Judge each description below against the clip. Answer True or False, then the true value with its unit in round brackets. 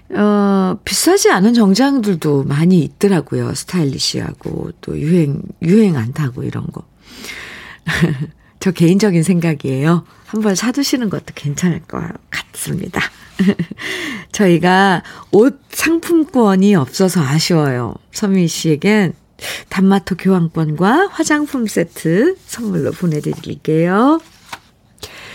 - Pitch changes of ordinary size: True (4.9 semitones)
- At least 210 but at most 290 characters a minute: True (240 characters per minute)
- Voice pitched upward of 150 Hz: True (185 Hz)